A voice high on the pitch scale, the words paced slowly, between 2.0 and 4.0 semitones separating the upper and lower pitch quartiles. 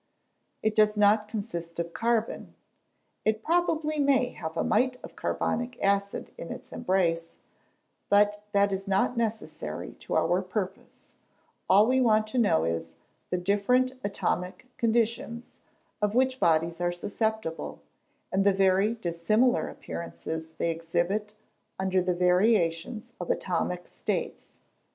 No: high, 205 Hz; slow, 130 wpm; average, 4.5 semitones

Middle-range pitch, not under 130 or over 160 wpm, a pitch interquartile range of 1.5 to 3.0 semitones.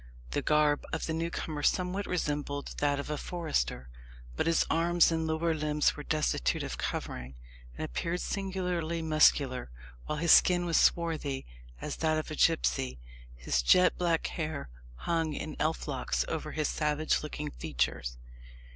Yes: medium, 155 Hz; average, 155 wpm; average, 2.7 semitones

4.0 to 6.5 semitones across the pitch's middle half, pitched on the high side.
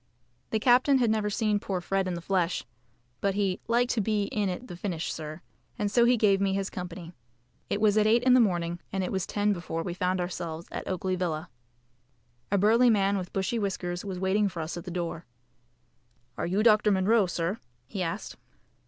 No: average, 3.1 semitones; high, 195 Hz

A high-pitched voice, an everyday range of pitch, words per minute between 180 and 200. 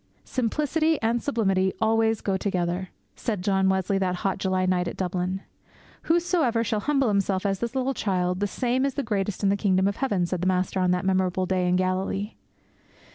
Yes: high, 195 Hz; average, 3.6 semitones; average, 190 wpm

